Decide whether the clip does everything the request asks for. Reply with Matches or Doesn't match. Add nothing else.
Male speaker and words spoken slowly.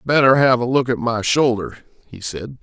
Doesn't match